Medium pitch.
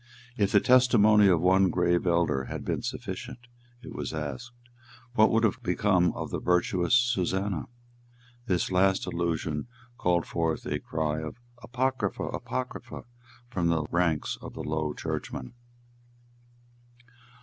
No: very low, 90 Hz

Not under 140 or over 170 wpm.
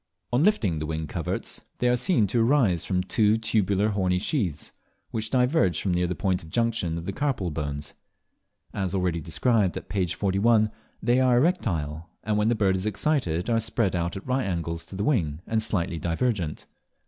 No: average, 190 wpm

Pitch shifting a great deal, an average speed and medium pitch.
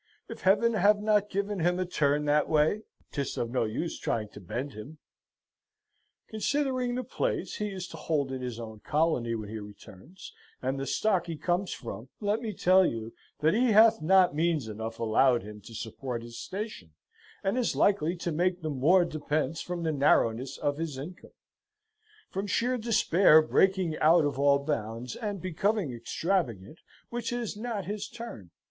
Yes: wide, 7.8 semitones; average, 175 wpm; medium, 160 Hz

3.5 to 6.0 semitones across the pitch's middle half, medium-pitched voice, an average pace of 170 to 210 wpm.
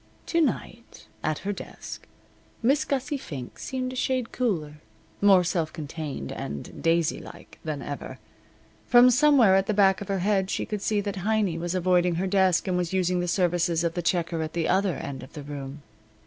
Yes: average, 4.0 semitones; medium, 180 Hz; average, 190 wpm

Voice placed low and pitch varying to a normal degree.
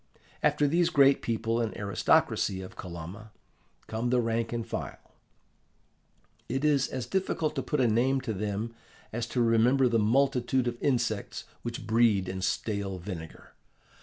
Yes: low, 115 Hz; average, 3.5 semitones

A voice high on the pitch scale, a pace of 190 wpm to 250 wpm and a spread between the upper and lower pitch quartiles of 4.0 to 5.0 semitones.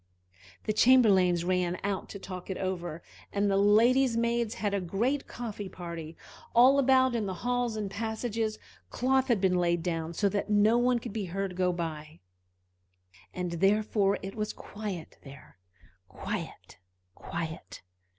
No: high, 200 Hz; average, 155 wpm; average, 4.3 semitones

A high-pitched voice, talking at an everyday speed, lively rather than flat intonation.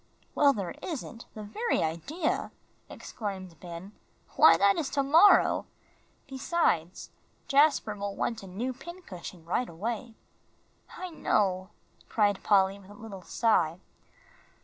No: high, 210 Hz; slow, 125 wpm; wide, 6.5 semitones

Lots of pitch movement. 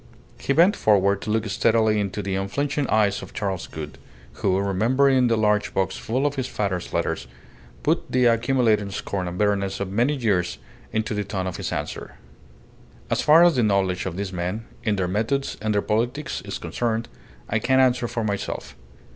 No: average, 3.8 semitones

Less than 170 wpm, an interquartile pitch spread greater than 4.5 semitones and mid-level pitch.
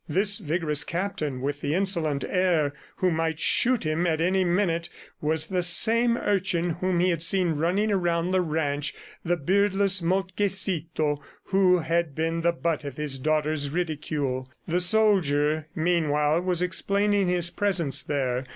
No: average, 150 wpm; average, 3.5 semitones; medium, 170 Hz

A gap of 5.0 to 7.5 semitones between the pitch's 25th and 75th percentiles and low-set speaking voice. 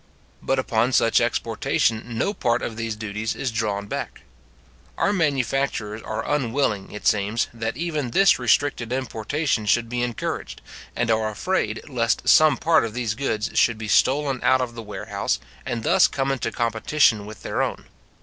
No: average, 3.6 semitones; low, 115 Hz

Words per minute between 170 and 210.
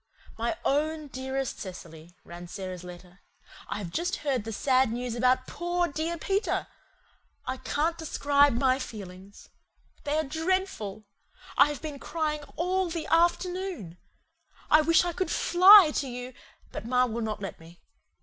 No: average, 150 wpm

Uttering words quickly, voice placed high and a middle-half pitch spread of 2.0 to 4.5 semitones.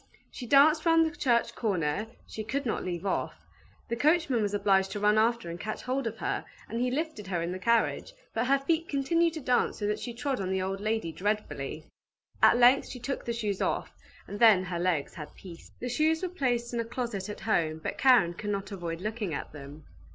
No: fast, 225 wpm; high, 225 Hz; average, 5.2 semitones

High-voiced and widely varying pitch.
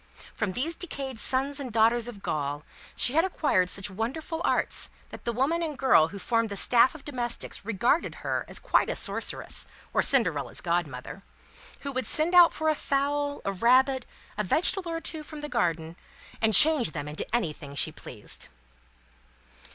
Yes: high, 245 Hz; wide, 7.6 semitones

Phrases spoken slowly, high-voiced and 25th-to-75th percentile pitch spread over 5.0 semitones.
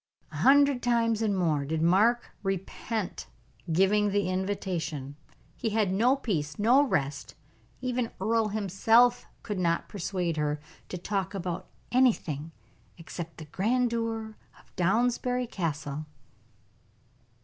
Yes: slow, 115 wpm; high, 200 Hz; wide, 5.4 semitones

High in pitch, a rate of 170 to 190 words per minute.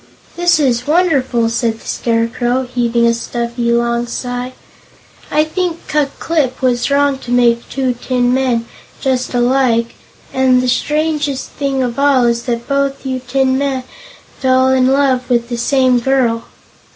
No: very high, 255 Hz; average, 150 wpm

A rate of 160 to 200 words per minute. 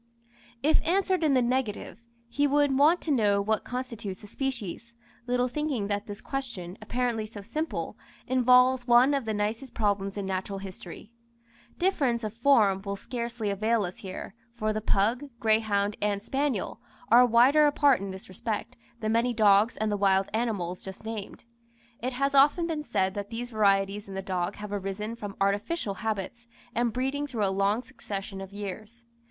Yes: average, 170 wpm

